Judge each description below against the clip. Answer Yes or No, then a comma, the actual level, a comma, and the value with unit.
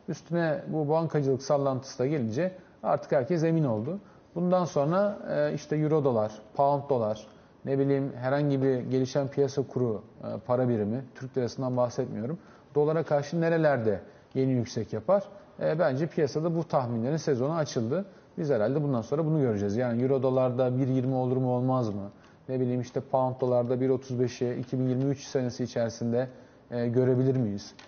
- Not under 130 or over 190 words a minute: Yes, fast, 140 wpm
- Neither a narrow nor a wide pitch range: Yes, average, 3.0 semitones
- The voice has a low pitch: Yes, low, 130 Hz